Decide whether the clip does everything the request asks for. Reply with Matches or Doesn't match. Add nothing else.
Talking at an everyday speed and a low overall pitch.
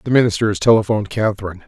Matches